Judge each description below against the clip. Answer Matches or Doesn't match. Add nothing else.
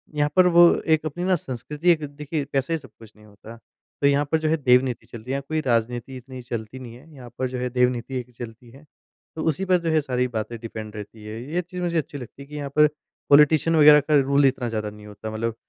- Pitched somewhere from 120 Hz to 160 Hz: Matches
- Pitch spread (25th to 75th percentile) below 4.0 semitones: Doesn't match